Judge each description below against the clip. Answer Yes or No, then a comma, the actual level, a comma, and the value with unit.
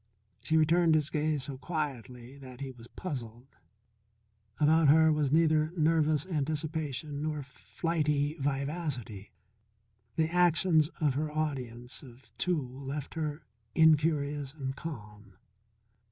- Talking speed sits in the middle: No, slow, 120 wpm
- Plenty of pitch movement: No, average, 3.0 semitones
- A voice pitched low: No, medium, 150 Hz